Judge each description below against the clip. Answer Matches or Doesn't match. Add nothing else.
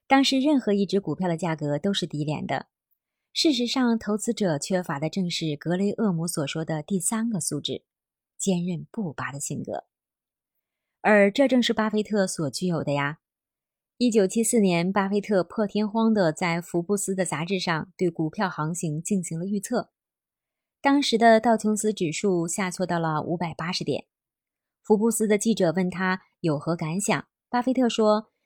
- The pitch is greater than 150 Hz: Matches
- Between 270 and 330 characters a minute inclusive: Doesn't match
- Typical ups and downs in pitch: Matches